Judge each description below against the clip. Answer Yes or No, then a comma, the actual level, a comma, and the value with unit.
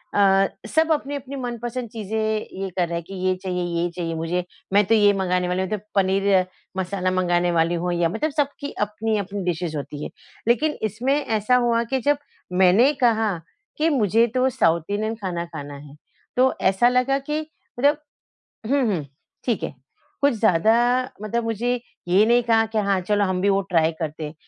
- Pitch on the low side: No, high, 205 Hz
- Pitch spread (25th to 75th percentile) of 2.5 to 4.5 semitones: No, average, 5.0 semitones